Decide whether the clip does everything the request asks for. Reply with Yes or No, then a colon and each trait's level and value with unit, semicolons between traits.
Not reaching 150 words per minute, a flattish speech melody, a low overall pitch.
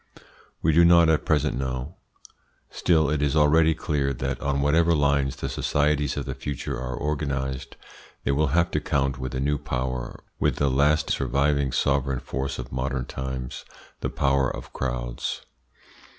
No: average, 165 wpm; narrow, 2.3 semitones; very low, 70 Hz